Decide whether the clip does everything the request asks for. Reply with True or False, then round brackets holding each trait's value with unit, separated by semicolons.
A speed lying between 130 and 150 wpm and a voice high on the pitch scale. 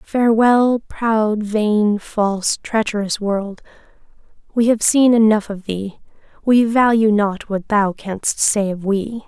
True (135 wpm; 215 Hz)